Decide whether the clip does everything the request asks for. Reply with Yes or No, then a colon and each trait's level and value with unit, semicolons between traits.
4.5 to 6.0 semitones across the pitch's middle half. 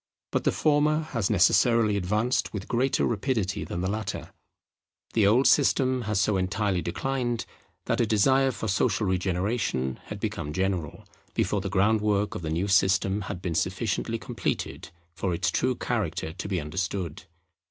No: average, 3.8 semitones